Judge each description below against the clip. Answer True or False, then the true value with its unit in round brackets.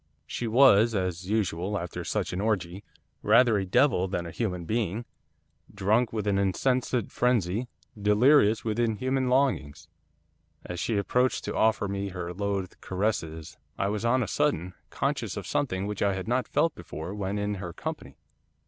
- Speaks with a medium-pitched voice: False (105 Hz)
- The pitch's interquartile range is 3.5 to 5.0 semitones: True (4.2 semitones)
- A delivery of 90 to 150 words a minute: False (165 wpm)